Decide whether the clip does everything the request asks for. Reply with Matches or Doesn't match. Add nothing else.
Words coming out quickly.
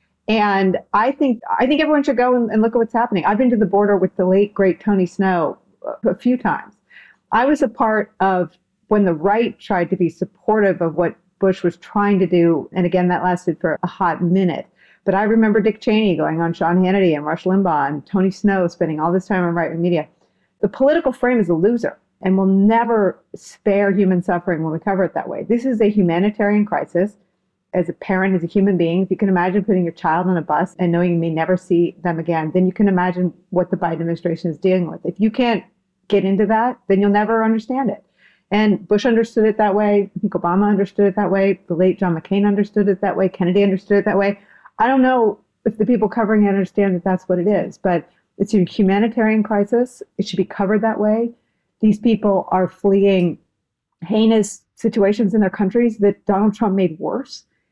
Matches